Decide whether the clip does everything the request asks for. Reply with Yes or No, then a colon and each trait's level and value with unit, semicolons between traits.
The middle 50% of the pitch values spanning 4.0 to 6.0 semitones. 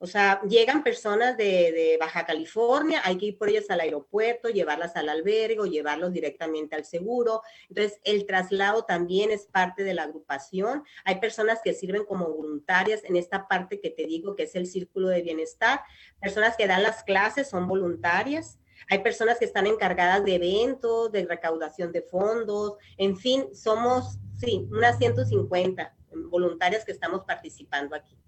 Yes: average, 4.4 semitones